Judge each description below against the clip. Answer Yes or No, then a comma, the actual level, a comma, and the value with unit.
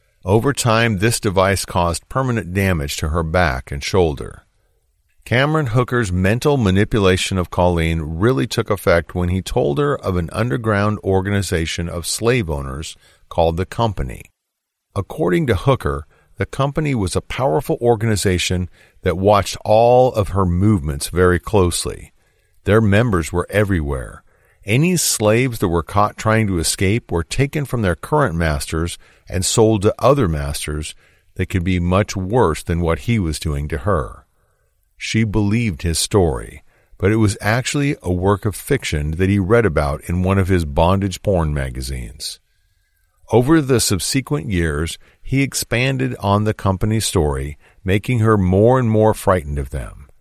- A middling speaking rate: Yes, average, 155 wpm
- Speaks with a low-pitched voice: Yes, very low, 95 Hz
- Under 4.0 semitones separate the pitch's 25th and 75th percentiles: No, average, 4.7 semitones